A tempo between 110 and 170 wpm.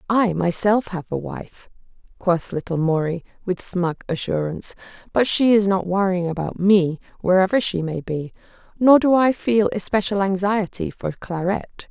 Yes: average, 150 wpm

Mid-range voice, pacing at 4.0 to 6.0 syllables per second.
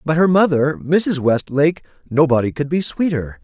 Yes: medium, 150 Hz; 4.9 syllables/s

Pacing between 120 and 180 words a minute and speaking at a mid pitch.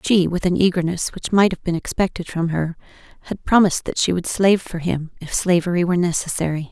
No: fast, 205 wpm; medium, 175 Hz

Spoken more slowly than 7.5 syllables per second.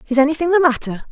No: 7.9 syllables/s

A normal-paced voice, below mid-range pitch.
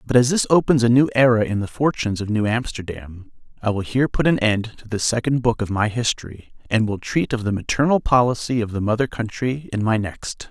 No: fast, 230 wpm; low, 115 Hz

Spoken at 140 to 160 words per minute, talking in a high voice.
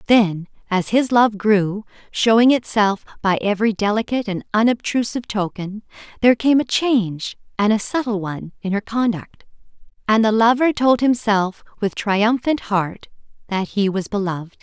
Yes: average, 150 wpm; high, 215 Hz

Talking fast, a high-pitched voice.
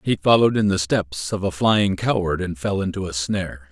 No: fast, 225 wpm; very low, 95 Hz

